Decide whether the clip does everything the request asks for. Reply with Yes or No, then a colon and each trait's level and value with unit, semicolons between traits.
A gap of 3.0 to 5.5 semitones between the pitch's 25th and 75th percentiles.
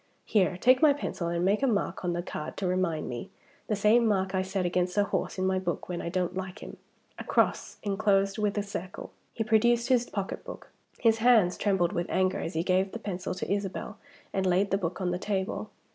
No: narrow, 2.6 semitones